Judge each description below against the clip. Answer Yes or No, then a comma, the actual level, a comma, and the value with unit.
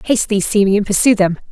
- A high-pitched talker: Yes, high, 205 Hz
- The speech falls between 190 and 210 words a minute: Yes, average, 200 wpm